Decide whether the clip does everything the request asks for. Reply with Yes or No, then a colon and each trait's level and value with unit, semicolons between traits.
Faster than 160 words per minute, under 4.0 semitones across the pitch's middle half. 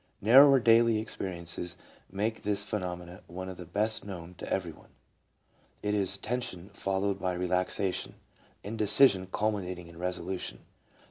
No: slow, 135 wpm; average, 3.0 semitones